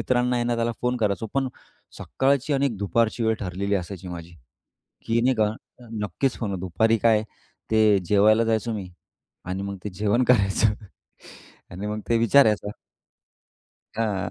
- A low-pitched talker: Yes, low, 110 Hz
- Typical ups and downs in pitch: Yes, average, 3.1 semitones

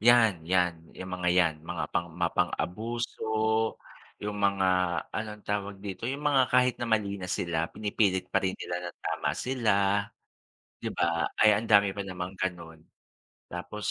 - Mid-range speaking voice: No, low, 100 Hz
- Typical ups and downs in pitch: Yes, average, 3.3 semitones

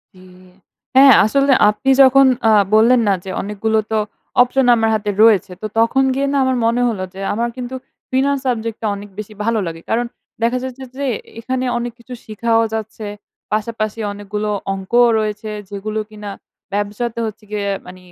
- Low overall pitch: No, high, 225 Hz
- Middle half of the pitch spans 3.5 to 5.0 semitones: No, average, 2.9 semitones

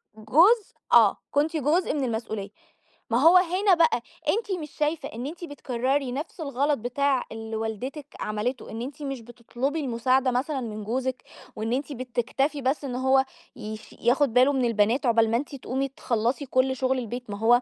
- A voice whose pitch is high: Yes, very high, 260 Hz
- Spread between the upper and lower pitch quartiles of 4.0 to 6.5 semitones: No, average, 3.5 semitones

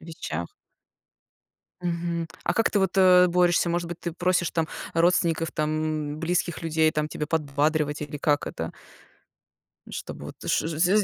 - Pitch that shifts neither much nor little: No, narrow, 2.3 semitones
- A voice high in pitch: No, medium, 165 Hz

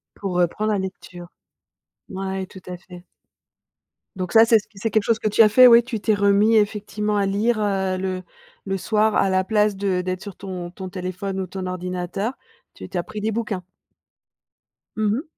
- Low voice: No, high, 195 Hz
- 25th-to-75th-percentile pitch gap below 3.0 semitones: Yes, narrow, 2.5 semitones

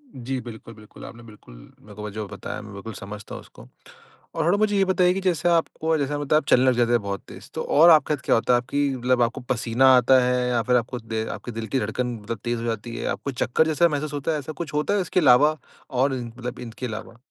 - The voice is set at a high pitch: No, low, 125 Hz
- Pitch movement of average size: Yes, average, 4.7 semitones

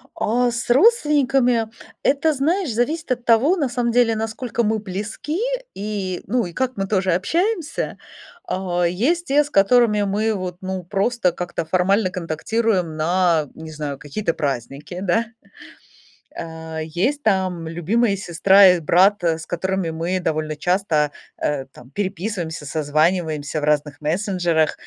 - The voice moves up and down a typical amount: No, wide, 6.2 semitones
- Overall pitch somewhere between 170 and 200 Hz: Yes, high, 190 Hz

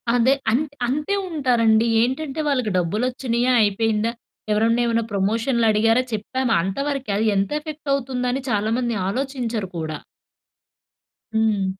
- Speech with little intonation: No, average, 3.4 semitones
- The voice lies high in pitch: Yes, high, 235 Hz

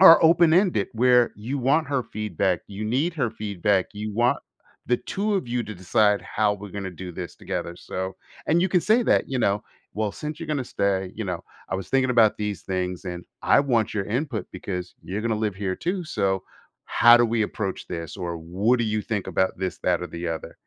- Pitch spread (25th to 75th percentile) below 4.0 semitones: No, average, 5.0 semitones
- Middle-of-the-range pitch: No, low, 105 Hz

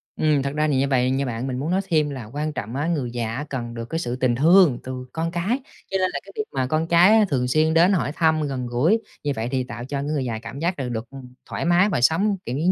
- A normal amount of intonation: Yes, average, 4.8 semitones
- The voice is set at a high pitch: No, medium, 140 Hz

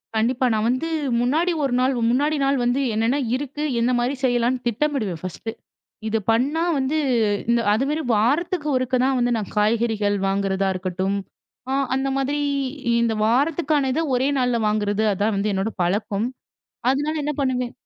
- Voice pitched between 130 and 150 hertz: No, high, 245 Hz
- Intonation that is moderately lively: Yes, average, 4.3 semitones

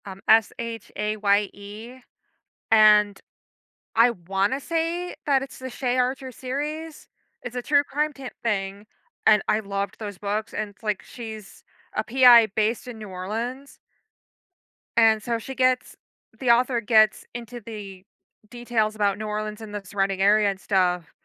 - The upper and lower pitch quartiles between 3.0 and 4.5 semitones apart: Yes, average, 3.4 semitones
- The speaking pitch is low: No, high, 220 Hz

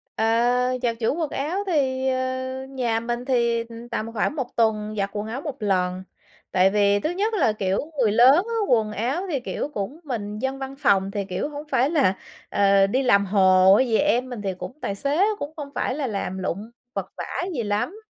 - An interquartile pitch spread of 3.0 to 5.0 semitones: Yes, average, 4.7 semitones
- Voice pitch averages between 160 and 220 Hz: No, high, 235 Hz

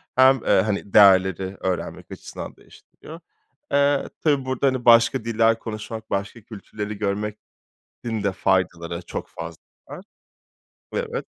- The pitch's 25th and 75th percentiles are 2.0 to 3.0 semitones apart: No, average, 3.9 semitones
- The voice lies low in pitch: Yes, low, 110 Hz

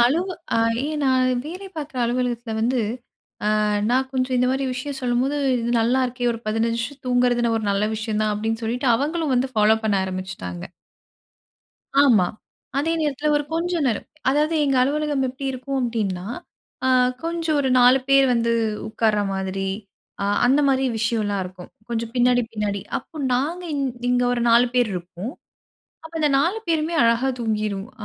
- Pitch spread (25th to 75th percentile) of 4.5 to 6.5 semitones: No, average, 3.7 semitones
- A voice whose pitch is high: Yes, high, 245 Hz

